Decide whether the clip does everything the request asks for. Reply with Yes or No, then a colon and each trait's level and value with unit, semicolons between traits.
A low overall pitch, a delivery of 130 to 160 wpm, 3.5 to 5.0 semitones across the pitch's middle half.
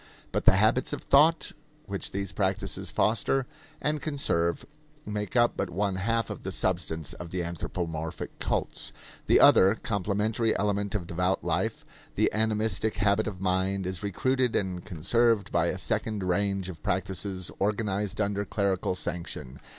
No: low, 100 Hz; average, 150 wpm; average, 2.8 semitones